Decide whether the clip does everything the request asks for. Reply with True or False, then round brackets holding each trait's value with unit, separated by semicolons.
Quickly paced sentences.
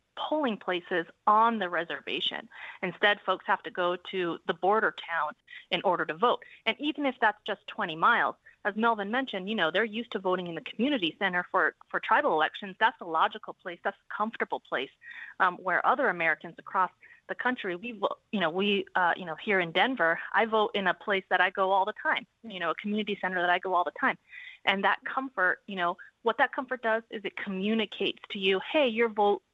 True (215 wpm)